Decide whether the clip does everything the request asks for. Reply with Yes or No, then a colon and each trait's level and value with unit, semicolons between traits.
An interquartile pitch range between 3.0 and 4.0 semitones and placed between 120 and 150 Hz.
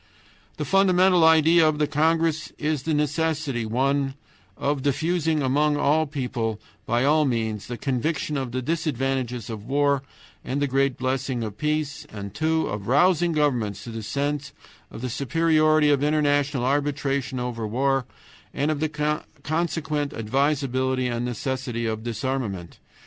Yes: average, 3.7 semitones; medium, 140 Hz